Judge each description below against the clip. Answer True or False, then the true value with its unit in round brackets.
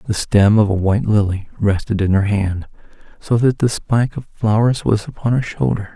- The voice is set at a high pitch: False (105 Hz)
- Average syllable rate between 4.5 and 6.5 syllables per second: True (5.1 syllables/s)